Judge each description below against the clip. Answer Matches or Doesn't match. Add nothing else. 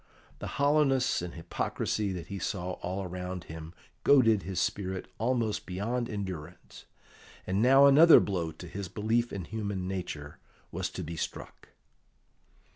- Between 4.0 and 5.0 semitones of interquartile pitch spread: Matches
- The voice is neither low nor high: Doesn't match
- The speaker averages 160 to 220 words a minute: Doesn't match